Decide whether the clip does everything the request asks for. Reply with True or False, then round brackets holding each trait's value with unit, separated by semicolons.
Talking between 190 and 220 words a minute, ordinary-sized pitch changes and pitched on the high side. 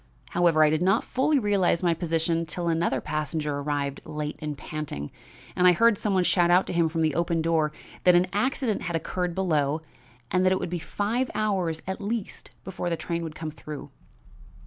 False (200 wpm; 3.2 semitones; 170 Hz)